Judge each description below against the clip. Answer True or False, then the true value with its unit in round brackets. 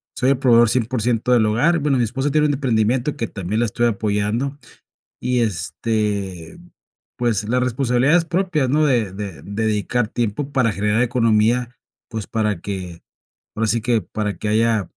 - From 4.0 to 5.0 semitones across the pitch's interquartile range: False (3.2 semitones)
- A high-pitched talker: False (115 Hz)